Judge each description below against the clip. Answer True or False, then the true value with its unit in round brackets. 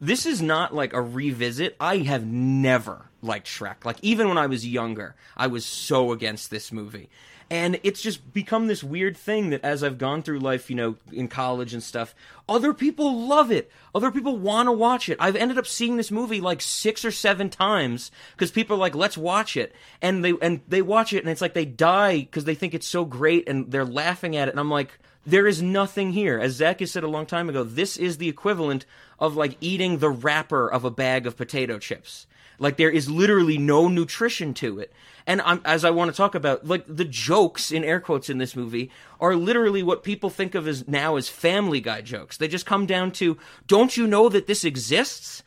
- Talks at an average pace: False (225 wpm)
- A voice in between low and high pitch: True (165 Hz)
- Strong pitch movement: True (6.7 semitones)